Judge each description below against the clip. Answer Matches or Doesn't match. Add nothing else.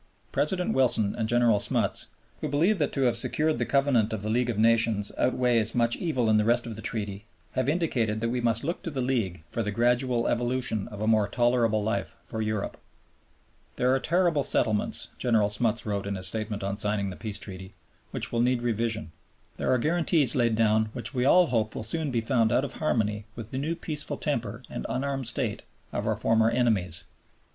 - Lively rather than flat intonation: Doesn't match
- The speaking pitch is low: Matches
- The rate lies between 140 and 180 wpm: Doesn't match